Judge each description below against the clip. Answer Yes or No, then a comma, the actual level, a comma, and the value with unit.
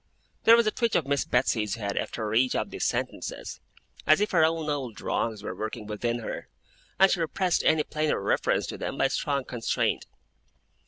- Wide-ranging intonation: Yes, wide, 6.5 semitones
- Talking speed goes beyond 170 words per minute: Yes, average, 190 wpm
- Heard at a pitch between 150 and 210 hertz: No, medium, 140 Hz